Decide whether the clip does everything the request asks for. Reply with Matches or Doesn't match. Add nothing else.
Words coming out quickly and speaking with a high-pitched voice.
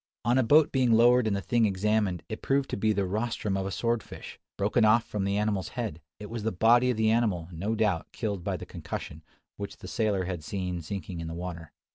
Doesn't match